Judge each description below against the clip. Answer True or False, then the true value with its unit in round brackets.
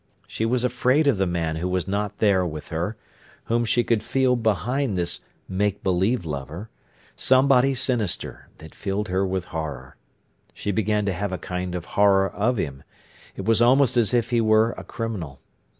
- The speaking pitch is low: True (105 Hz)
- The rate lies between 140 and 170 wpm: False (180 wpm)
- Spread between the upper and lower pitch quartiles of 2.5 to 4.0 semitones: False (4.8 semitones)